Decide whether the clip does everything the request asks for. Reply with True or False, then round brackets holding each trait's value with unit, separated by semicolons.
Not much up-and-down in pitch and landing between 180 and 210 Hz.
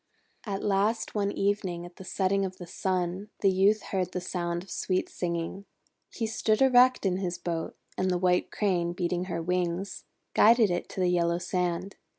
True (2.2 semitones; 185 Hz)